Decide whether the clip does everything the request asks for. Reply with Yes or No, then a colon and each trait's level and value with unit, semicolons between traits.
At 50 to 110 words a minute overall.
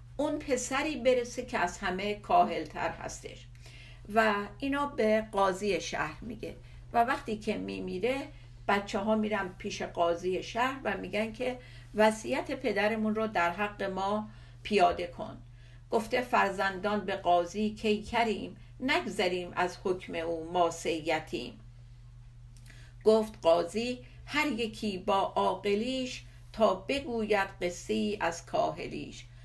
No: average, 120 wpm